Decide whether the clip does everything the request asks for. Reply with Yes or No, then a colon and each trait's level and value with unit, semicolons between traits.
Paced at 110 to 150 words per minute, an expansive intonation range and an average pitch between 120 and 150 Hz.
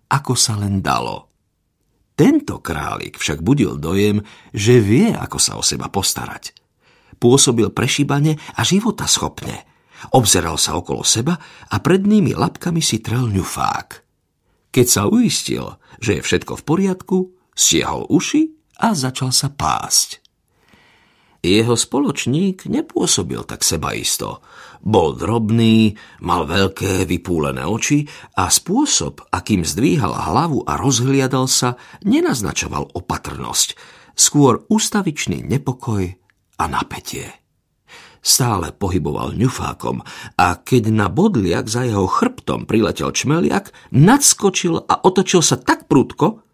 Yes: average, 115 wpm; wide, 8.6 semitones; low, 130 Hz